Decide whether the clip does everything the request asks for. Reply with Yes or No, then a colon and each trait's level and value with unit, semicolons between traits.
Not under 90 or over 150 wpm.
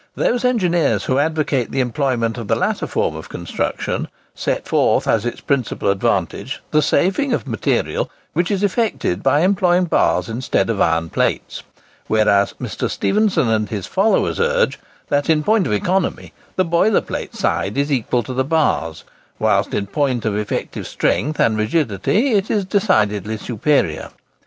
No: average, 160 wpm